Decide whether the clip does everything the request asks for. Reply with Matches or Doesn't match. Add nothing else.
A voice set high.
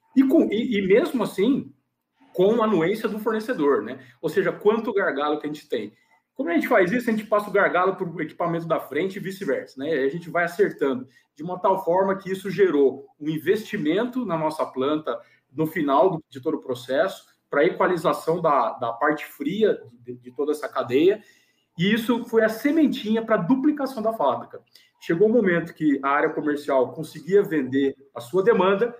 Doesn't match